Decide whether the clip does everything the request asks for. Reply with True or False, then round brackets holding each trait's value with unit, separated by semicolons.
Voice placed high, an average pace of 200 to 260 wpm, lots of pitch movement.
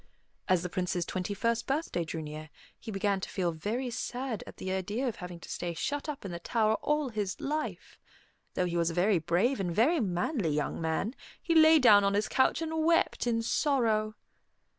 True (210 Hz; 205 wpm; 6.4 semitones)